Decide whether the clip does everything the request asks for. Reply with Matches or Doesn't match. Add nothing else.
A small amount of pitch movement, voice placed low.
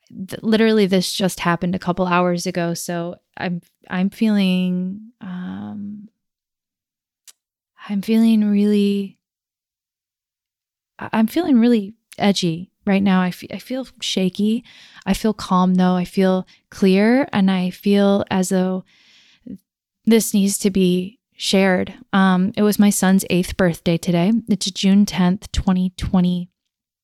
Doesn't match